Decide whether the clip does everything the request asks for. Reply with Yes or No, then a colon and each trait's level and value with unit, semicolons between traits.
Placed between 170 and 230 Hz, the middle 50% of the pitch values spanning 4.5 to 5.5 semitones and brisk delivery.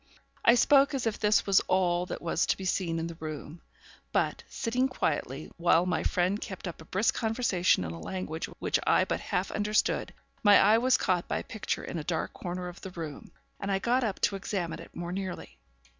No: medium, 185 Hz; average, 3.7 semitones; fast, 215 wpm